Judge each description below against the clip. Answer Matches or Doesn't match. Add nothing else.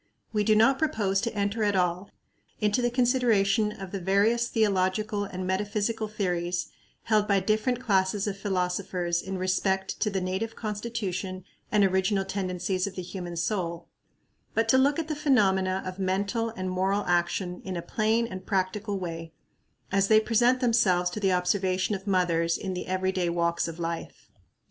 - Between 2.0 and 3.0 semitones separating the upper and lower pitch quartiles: Matches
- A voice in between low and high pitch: Doesn't match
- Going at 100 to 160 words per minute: Doesn't match